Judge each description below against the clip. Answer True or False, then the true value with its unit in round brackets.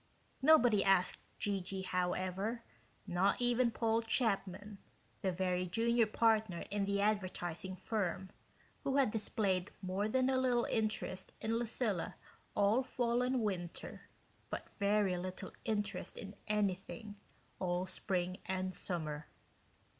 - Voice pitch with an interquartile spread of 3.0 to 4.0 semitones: True (3.4 semitones)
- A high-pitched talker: True (200 Hz)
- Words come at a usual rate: False (120 wpm)